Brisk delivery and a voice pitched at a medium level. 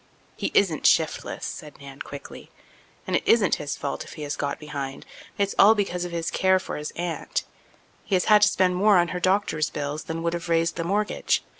Yes: fast, 210 wpm; medium, 170 Hz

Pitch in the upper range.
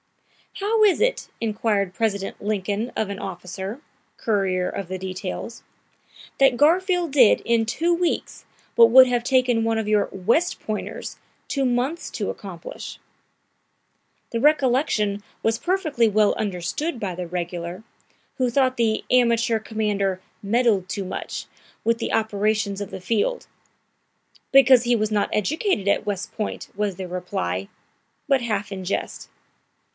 Yes: high, 220 Hz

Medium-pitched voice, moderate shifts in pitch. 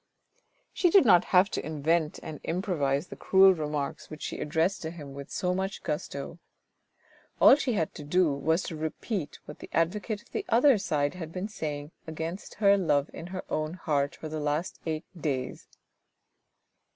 Yes: medium, 160 Hz; average, 3.9 semitones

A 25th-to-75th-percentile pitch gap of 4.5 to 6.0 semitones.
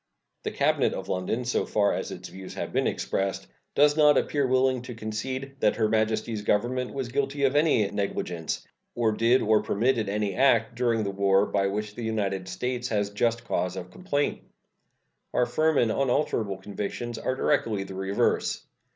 No: average, 4.1 semitones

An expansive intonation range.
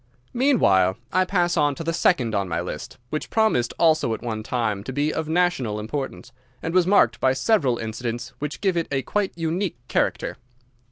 Yes: wide, 7.0 semitones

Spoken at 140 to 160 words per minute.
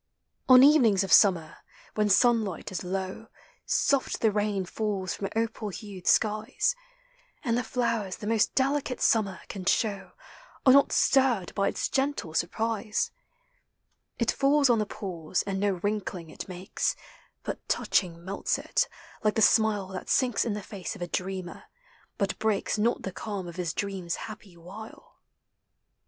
Yes: average, 150 wpm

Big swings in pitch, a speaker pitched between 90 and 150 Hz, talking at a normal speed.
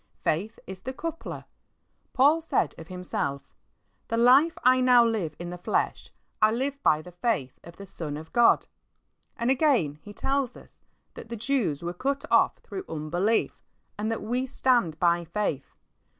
No: wide, 7.0 semitones; high, 220 Hz; average, 165 wpm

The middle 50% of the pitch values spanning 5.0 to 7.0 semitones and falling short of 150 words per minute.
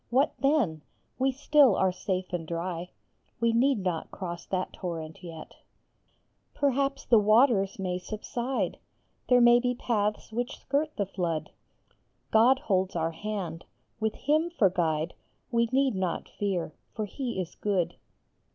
Yes: wide, 5.6 semitones; average, 140 wpm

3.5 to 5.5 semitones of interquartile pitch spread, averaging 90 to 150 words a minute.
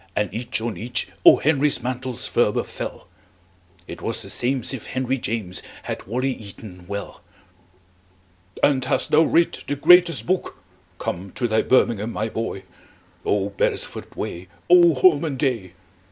Yes: average, 4.6 semitones; average, 140 wpm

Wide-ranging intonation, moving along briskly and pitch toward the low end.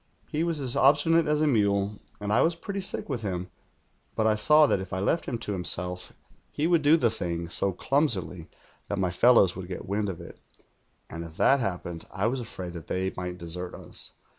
Yes: wide, 7.6 semitones; fast, 215 wpm; low, 100 Hz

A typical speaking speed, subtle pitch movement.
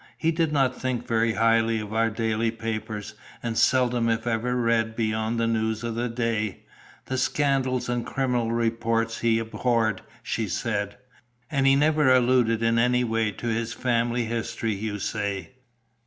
Yes: average, 160 wpm; narrow, 1.7 semitones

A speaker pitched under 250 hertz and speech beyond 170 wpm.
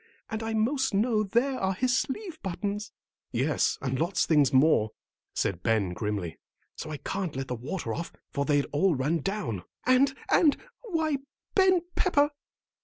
No: high, 190 Hz; average, 165 wpm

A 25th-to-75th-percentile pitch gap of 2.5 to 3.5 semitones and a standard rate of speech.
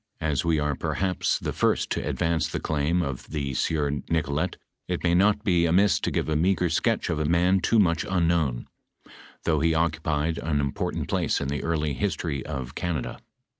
Yes: average, 2.9 semitones; average, 185 wpm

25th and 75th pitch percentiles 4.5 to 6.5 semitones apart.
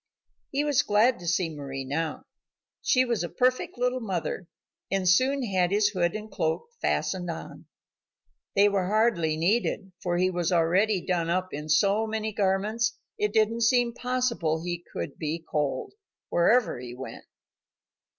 Yes: average, 4.8 semitones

